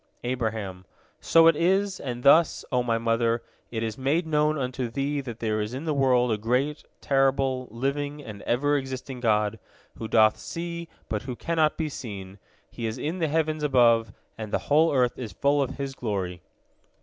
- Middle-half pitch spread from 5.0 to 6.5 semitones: No, average, 4.4 semitones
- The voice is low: Yes, low, 130 Hz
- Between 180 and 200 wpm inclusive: Yes, average, 185 wpm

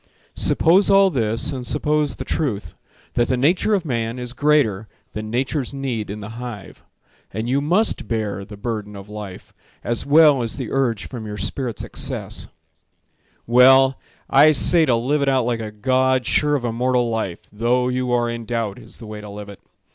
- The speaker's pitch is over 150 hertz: No, low, 120 Hz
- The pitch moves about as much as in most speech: Yes, average, 3.8 semitones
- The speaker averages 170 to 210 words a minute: Yes, average, 185 wpm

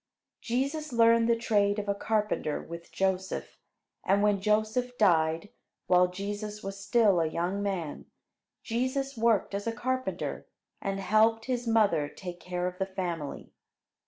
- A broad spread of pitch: No, average, 3.9 semitones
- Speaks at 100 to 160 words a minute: Yes, average, 145 wpm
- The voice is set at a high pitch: Yes, high, 205 Hz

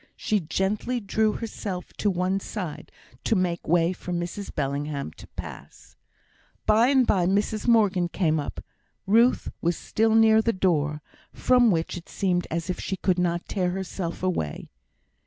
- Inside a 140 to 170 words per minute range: Yes, average, 155 wpm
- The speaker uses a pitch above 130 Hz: Yes, medium, 185 Hz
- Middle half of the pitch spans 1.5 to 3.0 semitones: No, average, 3.9 semitones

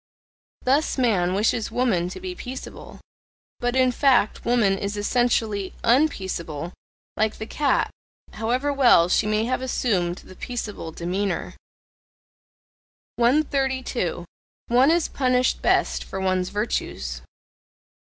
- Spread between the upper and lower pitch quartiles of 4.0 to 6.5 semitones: Yes, average, 5.2 semitones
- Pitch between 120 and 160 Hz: No, high, 230 Hz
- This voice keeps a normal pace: No, slow, 115 wpm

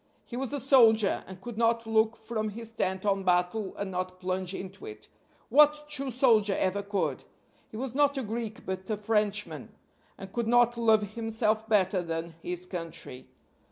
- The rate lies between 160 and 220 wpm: Yes, average, 175 wpm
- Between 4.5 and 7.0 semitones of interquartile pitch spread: No, average, 3.7 semitones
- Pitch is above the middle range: Yes, high, 215 Hz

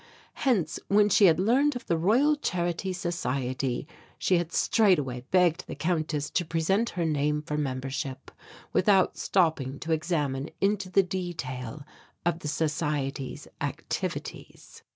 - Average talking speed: No, slow, 130 wpm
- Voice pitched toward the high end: No, medium, 165 Hz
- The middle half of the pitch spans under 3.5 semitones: No, average, 4.6 semitones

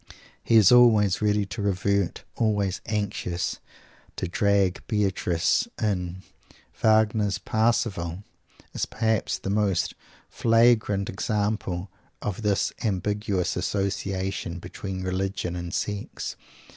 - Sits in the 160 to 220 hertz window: No, low, 100 Hz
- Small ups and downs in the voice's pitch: Yes, narrow, 2.3 semitones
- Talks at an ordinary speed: No, slow, 100 wpm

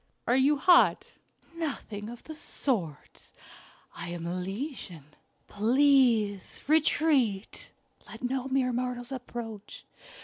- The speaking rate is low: Yes, slow, 100 wpm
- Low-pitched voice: No, high, 245 Hz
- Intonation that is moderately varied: Yes, average, 4.9 semitones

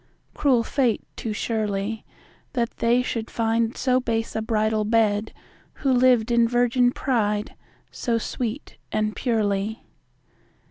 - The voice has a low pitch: No, high, 230 Hz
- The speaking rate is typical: No, slow, 125 wpm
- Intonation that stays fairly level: Yes, narrow, 2.1 semitones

